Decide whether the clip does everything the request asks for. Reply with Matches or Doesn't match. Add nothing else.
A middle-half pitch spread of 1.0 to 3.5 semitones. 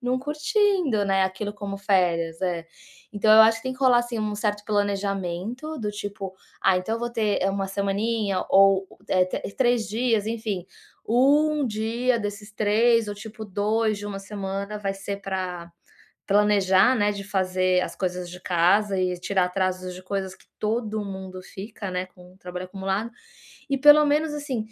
Matches